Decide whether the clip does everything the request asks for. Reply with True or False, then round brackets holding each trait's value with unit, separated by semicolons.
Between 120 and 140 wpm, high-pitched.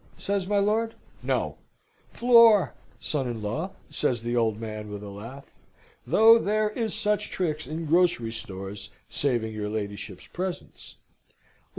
False (135 wpm; 140 Hz)